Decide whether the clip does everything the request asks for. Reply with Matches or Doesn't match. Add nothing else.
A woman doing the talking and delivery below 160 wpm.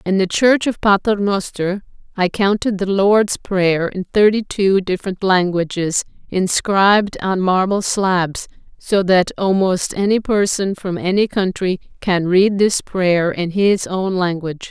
Matches